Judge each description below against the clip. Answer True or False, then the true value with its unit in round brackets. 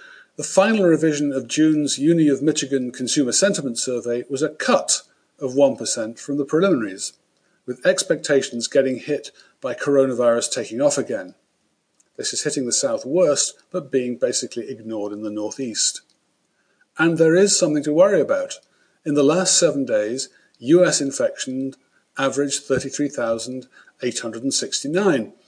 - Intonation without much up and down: False (4.4 semitones)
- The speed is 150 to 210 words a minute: False (135 wpm)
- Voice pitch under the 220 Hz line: True (140 Hz)